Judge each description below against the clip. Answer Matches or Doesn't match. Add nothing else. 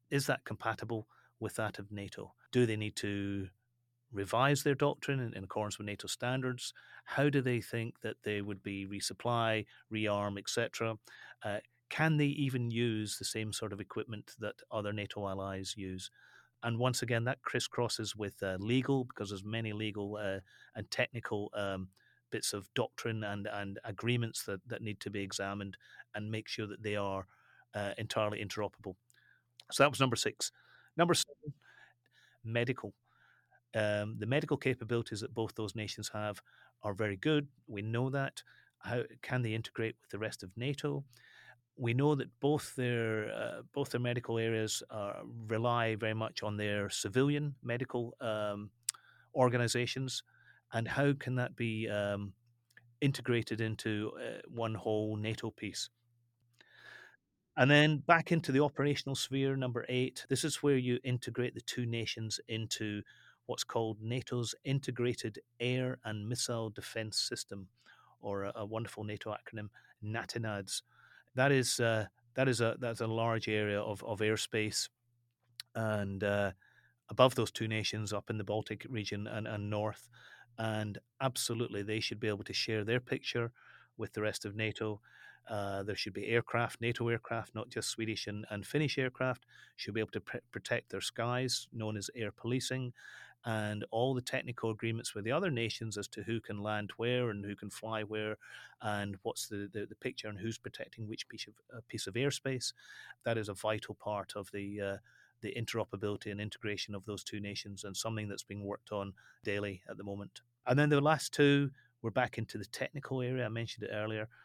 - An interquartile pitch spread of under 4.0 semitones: Matches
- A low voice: Matches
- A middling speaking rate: Matches